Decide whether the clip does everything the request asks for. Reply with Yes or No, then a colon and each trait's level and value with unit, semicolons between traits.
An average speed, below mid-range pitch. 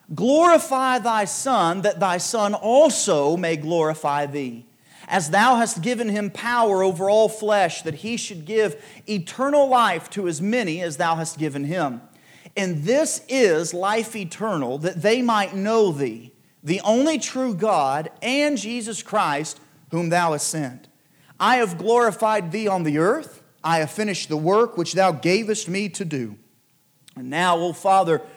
No: average, 165 wpm; high, 195 Hz